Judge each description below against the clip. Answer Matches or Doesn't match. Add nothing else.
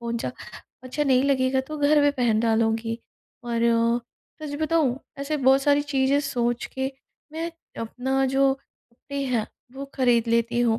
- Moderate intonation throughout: Matches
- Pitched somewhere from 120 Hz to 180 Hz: Doesn't match